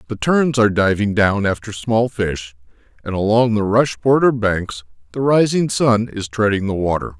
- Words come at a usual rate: Yes, average, 175 wpm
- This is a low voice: Yes, low, 110 Hz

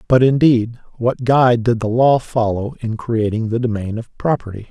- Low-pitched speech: Yes, low, 120 Hz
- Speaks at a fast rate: No, average, 180 wpm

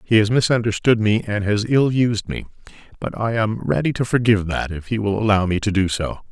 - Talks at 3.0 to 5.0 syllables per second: No, 5.5 syllables/s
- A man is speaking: Yes, male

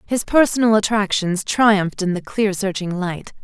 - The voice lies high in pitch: Yes, high, 200 Hz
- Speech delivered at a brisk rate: No, average, 155 wpm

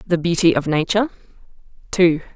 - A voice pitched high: No, medium, 170 Hz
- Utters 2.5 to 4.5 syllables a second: No, 6.1 syllables/s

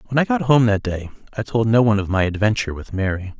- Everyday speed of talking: No, fast, 265 wpm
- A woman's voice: No, male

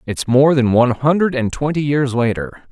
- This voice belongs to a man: Yes, male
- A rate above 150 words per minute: Yes, average, 200 wpm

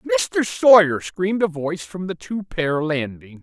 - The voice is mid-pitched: Yes, medium, 165 Hz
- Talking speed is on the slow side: No, average, 175 wpm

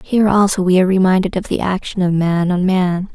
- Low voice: No, medium, 185 Hz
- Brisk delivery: Yes, fast, 230 wpm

